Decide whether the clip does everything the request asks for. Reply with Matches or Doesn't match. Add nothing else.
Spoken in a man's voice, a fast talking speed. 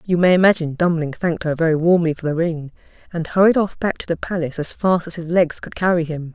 Doesn't match